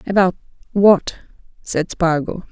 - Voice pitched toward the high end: No, medium, 180 Hz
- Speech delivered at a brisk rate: No, slow, 70 wpm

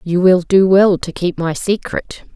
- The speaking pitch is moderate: Yes, medium, 180 Hz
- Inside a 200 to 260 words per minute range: Yes, fast, 205 wpm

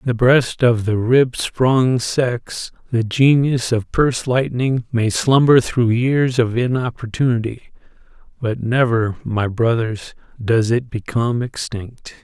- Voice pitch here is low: Yes, low, 120 Hz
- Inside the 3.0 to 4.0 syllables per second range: Yes, 3.9 syllables/s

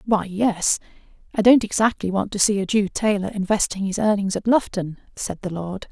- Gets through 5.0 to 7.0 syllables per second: Yes, 5.2 syllables/s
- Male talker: No, female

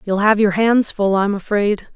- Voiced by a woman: Yes, female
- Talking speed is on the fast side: Yes, fast, 215 wpm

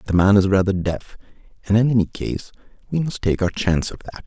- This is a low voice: Yes, low, 100 Hz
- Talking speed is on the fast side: Yes, fast, 225 wpm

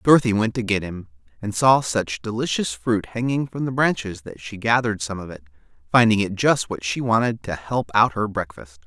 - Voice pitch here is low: Yes, low, 105 Hz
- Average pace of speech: No, fast, 210 wpm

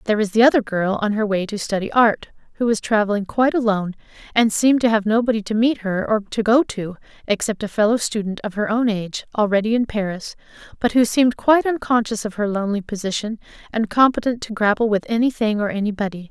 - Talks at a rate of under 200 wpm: No, fast, 205 wpm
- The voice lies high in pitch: Yes, high, 215 Hz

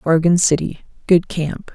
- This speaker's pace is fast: No, slow, 105 wpm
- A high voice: No, medium, 165 Hz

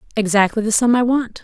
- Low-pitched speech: No, high, 225 Hz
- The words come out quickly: Yes, fast, 210 wpm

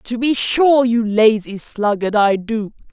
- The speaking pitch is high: Yes, high, 225 Hz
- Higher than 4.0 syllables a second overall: No, 3.7 syllables/s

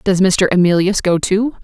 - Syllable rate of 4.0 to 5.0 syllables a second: Yes, 4.7 syllables/s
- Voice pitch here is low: No, high, 190 Hz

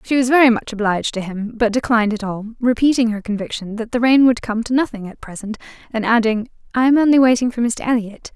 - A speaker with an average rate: No, fast, 230 wpm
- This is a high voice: Yes, high, 230 Hz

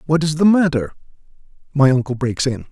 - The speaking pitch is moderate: Yes, medium, 145 Hz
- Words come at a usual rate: Yes, average, 175 wpm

